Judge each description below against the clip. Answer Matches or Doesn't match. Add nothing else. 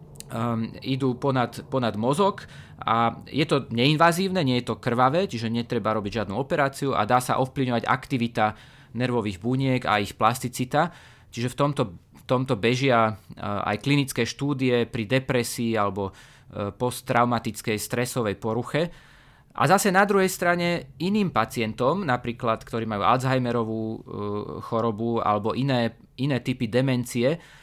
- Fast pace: Doesn't match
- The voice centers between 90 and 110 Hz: Doesn't match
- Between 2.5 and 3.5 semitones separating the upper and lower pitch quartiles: Matches